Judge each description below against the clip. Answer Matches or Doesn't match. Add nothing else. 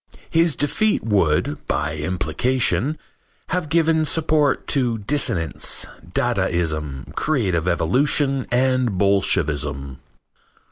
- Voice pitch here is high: Doesn't match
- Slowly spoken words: Matches